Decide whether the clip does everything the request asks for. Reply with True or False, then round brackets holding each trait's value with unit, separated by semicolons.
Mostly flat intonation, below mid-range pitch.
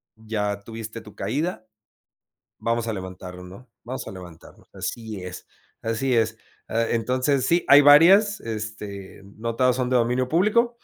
False (3.7 semitones; 115 Hz)